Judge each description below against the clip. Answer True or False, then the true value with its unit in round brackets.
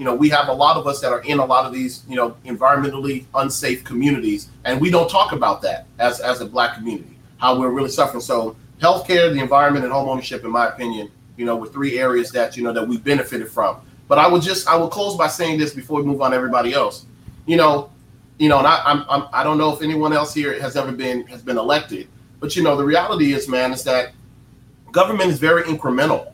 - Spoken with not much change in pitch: False (3.3 semitones)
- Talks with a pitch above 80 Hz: True (140 Hz)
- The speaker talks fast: True (245 wpm)